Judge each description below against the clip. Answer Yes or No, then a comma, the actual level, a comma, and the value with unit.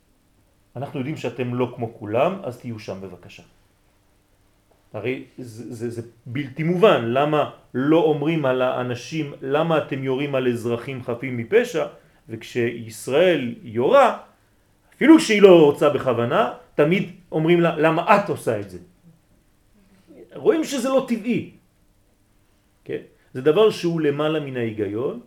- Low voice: Yes, low, 130 Hz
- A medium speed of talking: No, slow, 130 wpm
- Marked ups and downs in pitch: Yes, wide, 5.8 semitones